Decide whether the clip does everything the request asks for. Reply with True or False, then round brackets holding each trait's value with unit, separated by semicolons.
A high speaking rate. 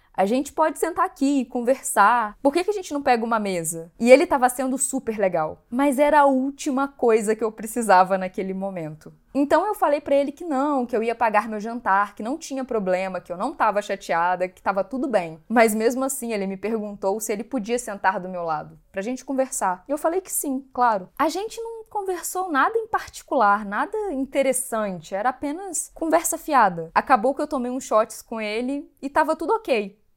True (210 wpm)